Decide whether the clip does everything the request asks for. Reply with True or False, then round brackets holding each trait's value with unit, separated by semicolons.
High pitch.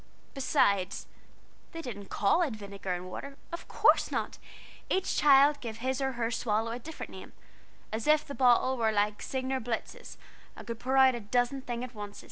True (245 Hz)